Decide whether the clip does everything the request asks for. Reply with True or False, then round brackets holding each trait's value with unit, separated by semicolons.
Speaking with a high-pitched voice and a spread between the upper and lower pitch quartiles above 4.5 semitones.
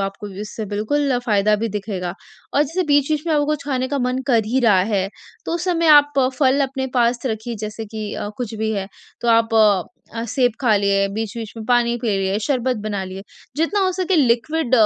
True (235 Hz; 5.1 semitones)